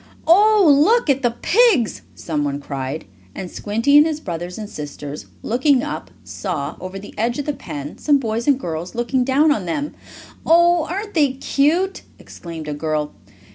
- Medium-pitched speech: No, high, 240 Hz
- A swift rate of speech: No, average, 170 wpm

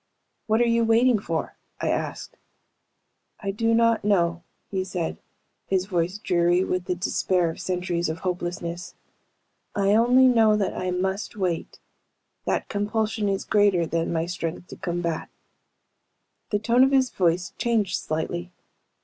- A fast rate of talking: No, average, 145 wpm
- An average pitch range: Yes, average, 3.8 semitones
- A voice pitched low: No, high, 190 Hz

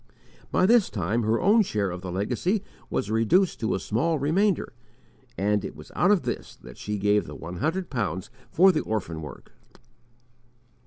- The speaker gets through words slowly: No, average, 175 wpm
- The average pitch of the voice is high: No, low, 115 Hz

